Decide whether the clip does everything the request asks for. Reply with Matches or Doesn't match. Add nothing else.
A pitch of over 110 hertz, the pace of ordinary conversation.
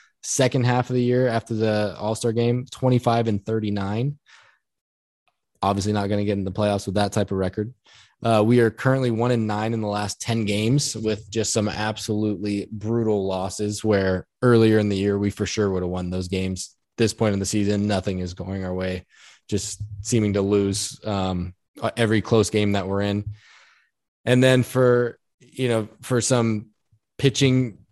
Doesn't match